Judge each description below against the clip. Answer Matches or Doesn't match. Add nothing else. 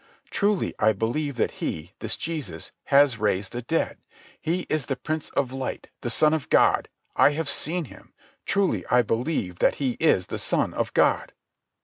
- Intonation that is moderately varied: Doesn't match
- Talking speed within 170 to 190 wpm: Matches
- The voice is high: Doesn't match